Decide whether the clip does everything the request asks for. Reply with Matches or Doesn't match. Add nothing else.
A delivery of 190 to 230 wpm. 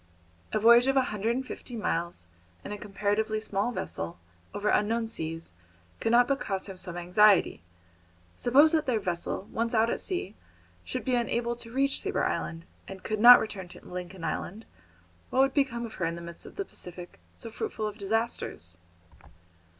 Doesn't match